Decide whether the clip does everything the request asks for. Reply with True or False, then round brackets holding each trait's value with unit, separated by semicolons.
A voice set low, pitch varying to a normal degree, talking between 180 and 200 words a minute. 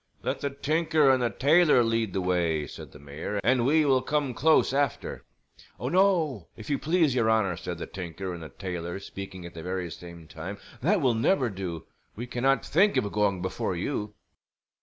False (110 Hz; 7.6 semitones; 195 wpm)